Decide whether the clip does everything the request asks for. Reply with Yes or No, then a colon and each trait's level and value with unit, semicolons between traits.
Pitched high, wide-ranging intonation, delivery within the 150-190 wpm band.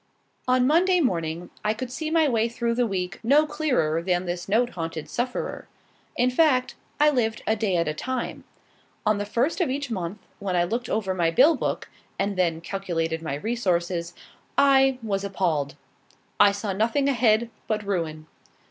Yes: high, 215 Hz; wide, 6.3 semitones; average, 175 wpm